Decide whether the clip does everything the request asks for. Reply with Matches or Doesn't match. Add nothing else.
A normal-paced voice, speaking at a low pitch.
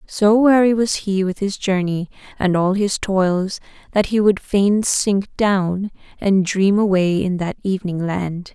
Doesn't match